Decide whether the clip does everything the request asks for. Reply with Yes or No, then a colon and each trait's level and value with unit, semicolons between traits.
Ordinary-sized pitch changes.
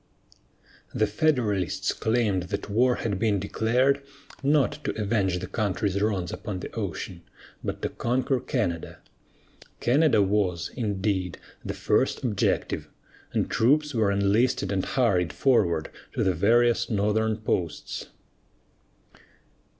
Yes: average, 4.0 semitones